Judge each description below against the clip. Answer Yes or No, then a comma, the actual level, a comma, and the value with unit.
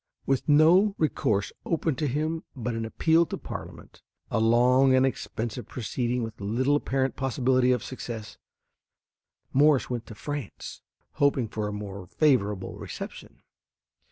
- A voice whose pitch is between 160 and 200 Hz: No, low, 125 Hz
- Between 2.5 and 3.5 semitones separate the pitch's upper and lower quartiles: No, average, 4.4 semitones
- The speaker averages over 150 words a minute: No, slow, 135 wpm